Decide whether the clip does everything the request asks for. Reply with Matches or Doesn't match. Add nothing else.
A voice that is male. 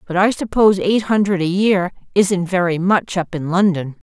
Doesn't match